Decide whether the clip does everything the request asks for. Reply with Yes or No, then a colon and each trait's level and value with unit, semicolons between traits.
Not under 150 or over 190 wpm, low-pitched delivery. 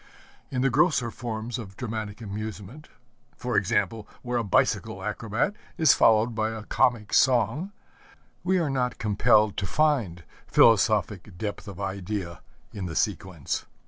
No: average, 140 wpm; low, 110 Hz